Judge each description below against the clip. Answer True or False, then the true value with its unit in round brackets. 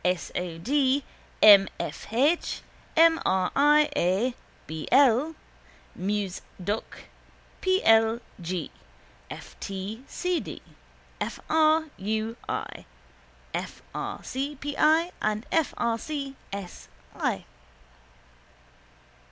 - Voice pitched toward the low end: False (235 Hz)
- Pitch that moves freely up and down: True (7.1 semitones)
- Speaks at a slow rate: True (110 wpm)